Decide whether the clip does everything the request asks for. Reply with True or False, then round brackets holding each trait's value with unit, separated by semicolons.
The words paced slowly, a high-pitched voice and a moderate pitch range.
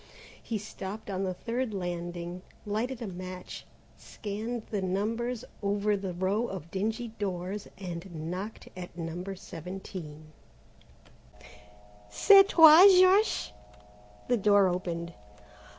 True (110 wpm; 195 Hz; 3.9 semitones)